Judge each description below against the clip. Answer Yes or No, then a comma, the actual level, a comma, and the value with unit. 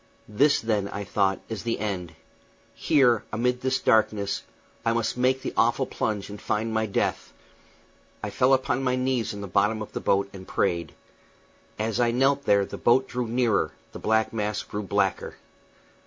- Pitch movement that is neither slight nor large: Yes, average, 3.6 semitones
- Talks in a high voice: No, low, 110 Hz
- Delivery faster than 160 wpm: Yes, average, 175 wpm